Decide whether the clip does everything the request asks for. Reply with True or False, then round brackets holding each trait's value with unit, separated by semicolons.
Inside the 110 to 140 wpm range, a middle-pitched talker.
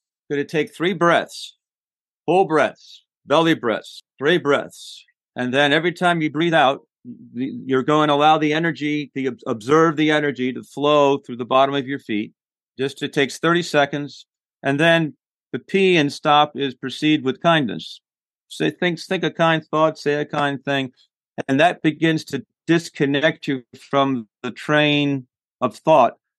False (165 wpm; 150 Hz)